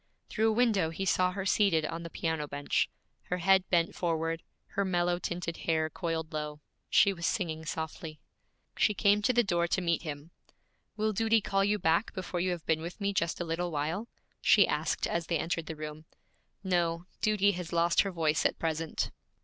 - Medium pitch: Yes, medium, 170 Hz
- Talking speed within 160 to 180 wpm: No, average, 195 wpm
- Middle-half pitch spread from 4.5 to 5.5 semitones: No, average, 3.1 semitones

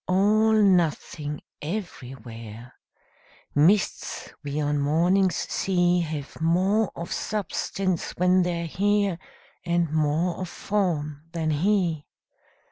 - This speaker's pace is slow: Yes, slow, 100 wpm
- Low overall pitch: No, medium, 170 Hz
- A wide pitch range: No, average, 4.2 semitones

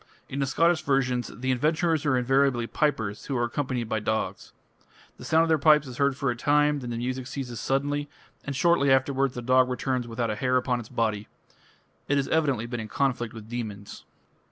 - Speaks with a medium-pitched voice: No, low, 130 Hz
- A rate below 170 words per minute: No, fast, 205 wpm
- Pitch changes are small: No, average, 3.0 semitones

